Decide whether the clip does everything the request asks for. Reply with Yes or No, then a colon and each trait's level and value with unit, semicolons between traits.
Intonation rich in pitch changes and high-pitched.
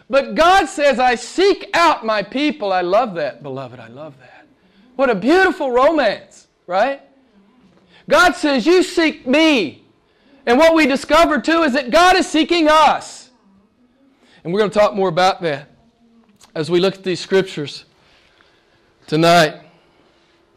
Yes: wide, 8.3 semitones; high, 245 Hz